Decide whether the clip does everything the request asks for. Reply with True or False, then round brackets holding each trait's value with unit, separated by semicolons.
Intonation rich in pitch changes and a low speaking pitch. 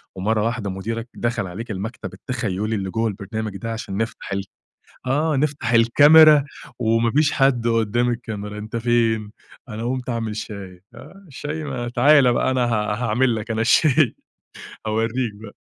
False (2.8 semitones; 115 Hz)